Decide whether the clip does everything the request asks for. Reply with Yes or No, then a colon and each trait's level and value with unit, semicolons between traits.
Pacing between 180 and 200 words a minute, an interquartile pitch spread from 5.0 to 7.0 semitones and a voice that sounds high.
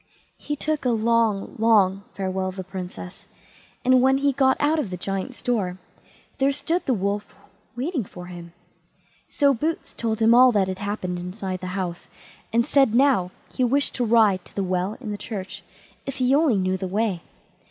Yes: average, 185 wpm; wide, 5.6 semitones; high, 215 Hz